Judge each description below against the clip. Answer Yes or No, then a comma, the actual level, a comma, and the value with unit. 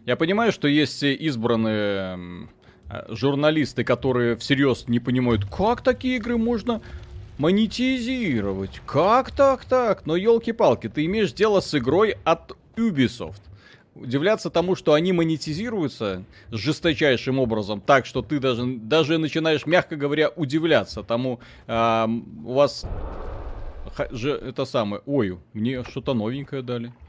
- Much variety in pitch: Yes, wide, 6.6 semitones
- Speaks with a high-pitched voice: No, medium, 140 Hz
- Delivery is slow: No, average, 120 wpm